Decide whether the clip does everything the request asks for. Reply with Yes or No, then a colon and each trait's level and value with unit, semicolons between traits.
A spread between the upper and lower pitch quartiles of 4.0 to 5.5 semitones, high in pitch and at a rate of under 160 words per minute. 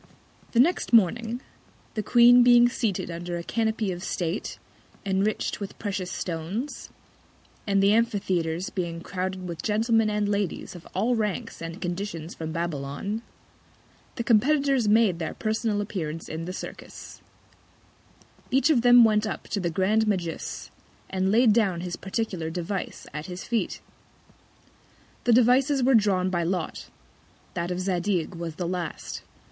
Yes: average, 4.5 semitones; high, 195 Hz; average, 145 wpm